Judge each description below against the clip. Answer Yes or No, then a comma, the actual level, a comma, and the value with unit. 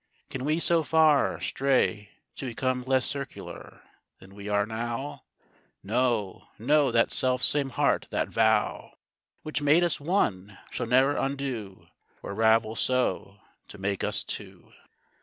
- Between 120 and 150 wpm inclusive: Yes, average, 140 wpm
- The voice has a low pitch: Yes, low, 125 Hz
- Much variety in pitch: No, average, 4.9 semitones